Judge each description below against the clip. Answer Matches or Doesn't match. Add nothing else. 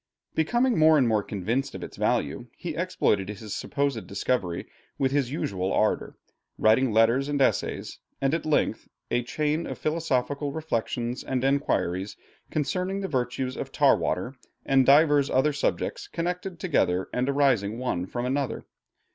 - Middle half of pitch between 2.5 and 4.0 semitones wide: Doesn't match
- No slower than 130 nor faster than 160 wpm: Matches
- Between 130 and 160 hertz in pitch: Matches